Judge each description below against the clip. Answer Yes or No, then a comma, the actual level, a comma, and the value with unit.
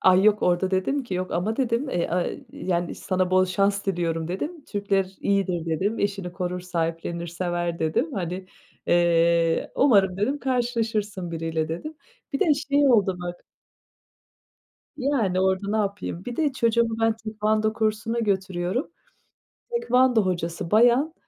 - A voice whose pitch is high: Yes, high, 195 Hz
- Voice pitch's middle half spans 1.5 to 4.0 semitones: No, average, 4.4 semitones